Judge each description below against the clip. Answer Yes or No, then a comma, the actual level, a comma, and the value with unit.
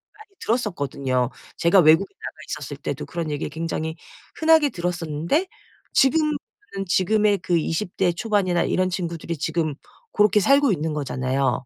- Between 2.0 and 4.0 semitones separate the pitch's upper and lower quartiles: No, average, 5.2 semitones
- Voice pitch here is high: No, medium, 175 Hz